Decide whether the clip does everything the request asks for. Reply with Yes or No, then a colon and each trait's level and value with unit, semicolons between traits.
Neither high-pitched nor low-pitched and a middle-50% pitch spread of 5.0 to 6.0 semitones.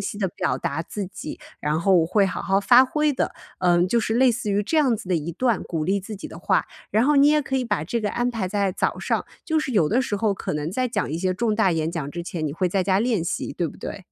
No: high, 200 Hz; wide, 5.6 semitones